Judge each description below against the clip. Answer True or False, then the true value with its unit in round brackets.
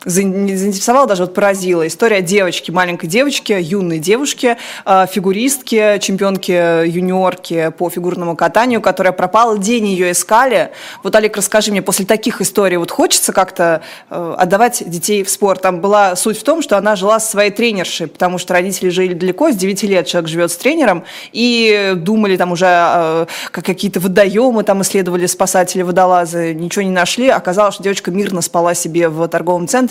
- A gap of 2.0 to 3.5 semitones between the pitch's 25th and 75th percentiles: True (2.8 semitones)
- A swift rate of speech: True (165 wpm)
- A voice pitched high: True (195 Hz)